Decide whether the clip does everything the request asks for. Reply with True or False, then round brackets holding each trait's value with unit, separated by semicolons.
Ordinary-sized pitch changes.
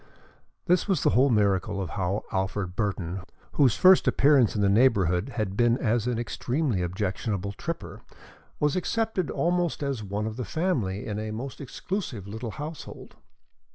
False (6.3 semitones)